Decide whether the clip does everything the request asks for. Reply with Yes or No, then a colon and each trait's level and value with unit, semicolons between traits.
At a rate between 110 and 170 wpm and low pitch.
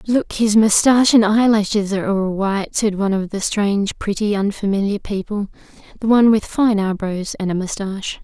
No: average, 160 wpm; high, 205 Hz